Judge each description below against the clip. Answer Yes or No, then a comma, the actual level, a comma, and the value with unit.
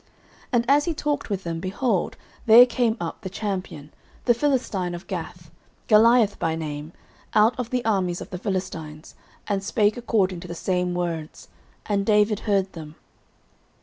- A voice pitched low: No, high, 195 Hz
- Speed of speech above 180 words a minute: No, average, 165 wpm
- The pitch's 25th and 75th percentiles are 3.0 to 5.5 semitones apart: Yes, average, 4.5 semitones